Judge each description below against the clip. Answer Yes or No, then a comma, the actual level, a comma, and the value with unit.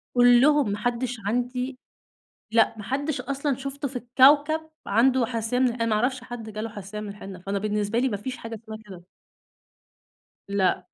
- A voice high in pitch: Yes, high, 240 Hz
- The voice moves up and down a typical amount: Yes, average, 3.7 semitones